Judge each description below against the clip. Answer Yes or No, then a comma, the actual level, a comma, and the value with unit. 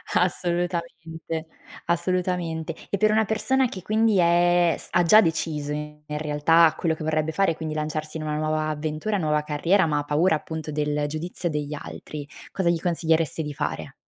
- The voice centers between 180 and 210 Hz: No, medium, 160 Hz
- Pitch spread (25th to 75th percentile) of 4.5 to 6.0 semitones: No, narrow, 2.5 semitones